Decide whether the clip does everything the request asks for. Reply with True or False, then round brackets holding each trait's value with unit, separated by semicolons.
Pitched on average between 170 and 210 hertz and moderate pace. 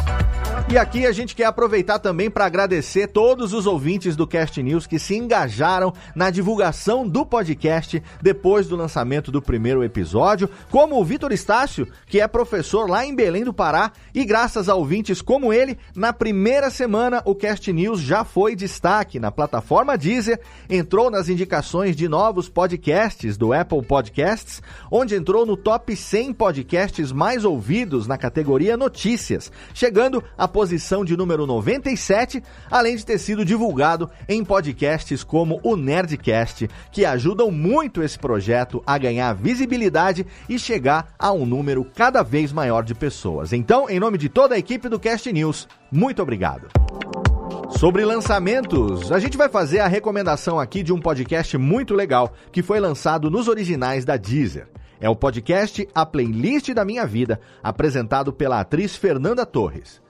True (185 Hz; 160 wpm)